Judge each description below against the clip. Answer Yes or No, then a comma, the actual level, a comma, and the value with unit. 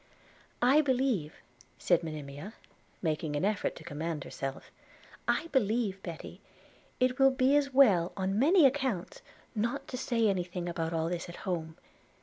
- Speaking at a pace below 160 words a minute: Yes, average, 150 wpm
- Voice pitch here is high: Yes, high, 195 Hz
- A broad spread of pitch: Yes, wide, 7.7 semitones